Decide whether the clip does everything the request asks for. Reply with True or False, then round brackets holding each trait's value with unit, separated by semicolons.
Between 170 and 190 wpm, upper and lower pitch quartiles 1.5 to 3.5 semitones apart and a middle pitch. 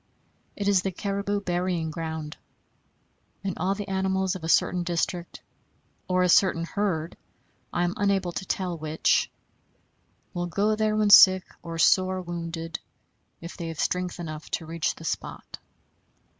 False (150 wpm; 2.5 semitones; 180 Hz)